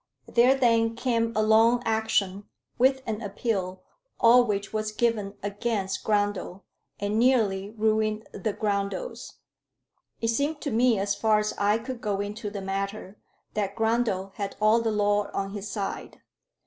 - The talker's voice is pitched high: Yes, high, 215 Hz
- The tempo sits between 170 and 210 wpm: No, average, 155 wpm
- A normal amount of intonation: No, narrow, 2.2 semitones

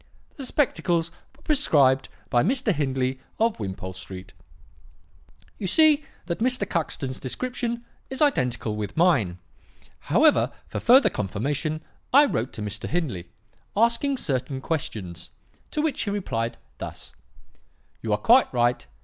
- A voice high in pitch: No, medium, 150 Hz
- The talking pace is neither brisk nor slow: No, slow, 130 wpm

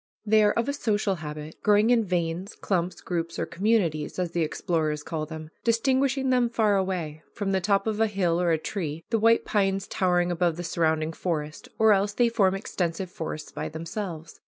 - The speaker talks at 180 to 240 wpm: Yes, average, 195 wpm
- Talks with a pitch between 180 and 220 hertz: Yes, medium, 185 Hz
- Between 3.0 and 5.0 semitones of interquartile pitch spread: Yes, average, 4.4 semitones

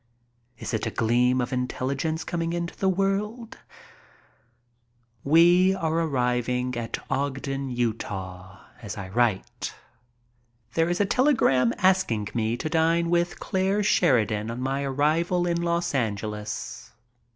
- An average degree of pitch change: No, wide, 6.6 semitones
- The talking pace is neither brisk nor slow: No, slow, 125 wpm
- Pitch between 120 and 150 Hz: Yes, low, 135 Hz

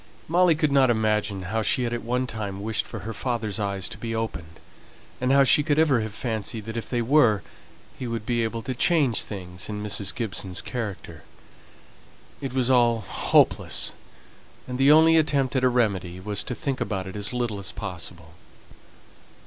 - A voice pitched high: No, low, 115 Hz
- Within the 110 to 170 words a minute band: No, average, 185 wpm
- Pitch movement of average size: Yes, average, 3.9 semitones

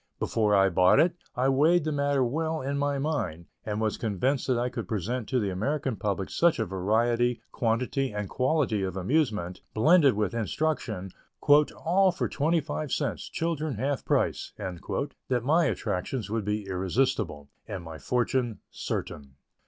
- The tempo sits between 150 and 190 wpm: Yes, average, 160 wpm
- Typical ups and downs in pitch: No, wide, 6.0 semitones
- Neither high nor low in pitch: No, low, 120 Hz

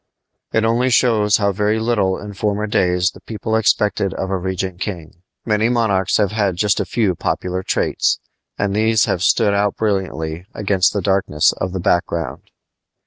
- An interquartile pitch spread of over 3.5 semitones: No, average, 2.7 semitones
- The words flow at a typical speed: Yes, average, 170 wpm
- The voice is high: No, low, 100 Hz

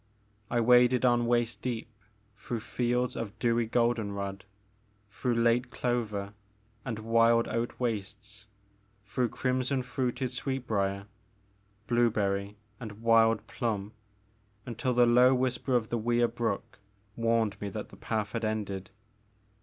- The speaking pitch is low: Yes, low, 115 Hz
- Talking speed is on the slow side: Yes, slow, 130 wpm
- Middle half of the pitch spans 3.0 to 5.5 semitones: No, narrow, 2.4 semitones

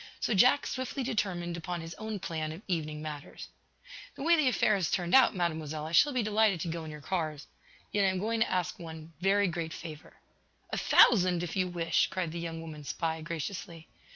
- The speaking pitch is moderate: Yes, medium, 175 Hz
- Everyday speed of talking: No, fast, 210 wpm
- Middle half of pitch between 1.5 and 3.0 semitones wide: No, average, 4.0 semitones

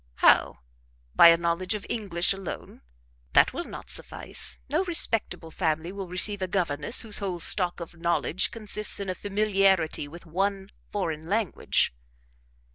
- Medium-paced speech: Yes, average, 145 wpm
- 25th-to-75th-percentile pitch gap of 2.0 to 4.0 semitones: Yes, average, 3.1 semitones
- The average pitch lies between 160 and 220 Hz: Yes, medium, 185 Hz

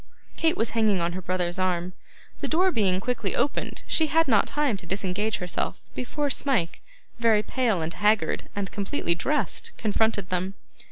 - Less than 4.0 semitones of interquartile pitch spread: No, average, 5.3 semitones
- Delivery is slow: No, average, 165 wpm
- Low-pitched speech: No, high, 210 Hz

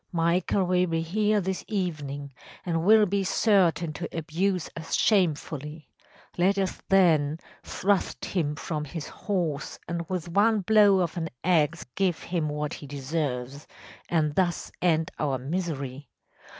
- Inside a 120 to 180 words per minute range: Yes, average, 140 wpm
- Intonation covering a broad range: No, average, 3.9 semitones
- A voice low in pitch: No, medium, 170 Hz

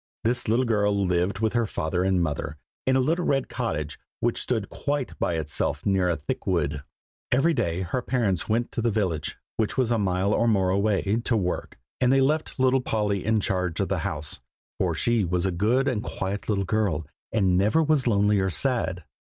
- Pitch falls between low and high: No, low, 105 Hz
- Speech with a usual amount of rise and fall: Yes, average, 4.7 semitones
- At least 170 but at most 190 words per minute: No, average, 200 wpm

